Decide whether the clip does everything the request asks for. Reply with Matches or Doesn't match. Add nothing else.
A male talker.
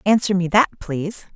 Doesn't match